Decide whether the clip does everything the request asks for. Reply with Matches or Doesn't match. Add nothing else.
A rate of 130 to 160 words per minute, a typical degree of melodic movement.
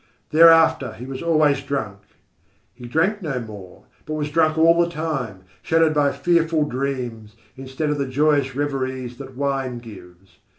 Matches